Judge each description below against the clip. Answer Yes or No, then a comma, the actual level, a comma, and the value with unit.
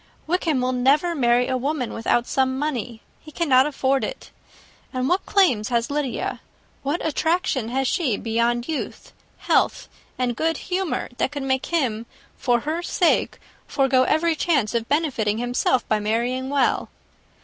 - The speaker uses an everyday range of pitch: Yes, average, 4.3 semitones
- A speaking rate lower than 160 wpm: Yes, average, 150 wpm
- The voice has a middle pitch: No, very high, 265 Hz